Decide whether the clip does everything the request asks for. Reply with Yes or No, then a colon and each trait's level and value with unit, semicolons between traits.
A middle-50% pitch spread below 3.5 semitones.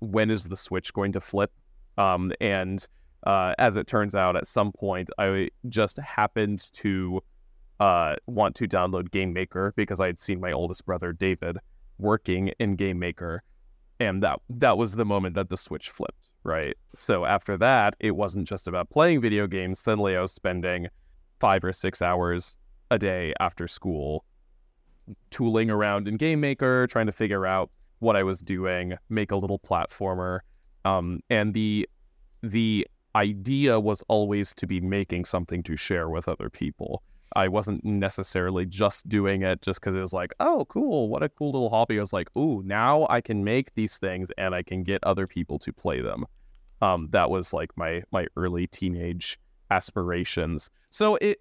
Yes: average, 2.8 semitones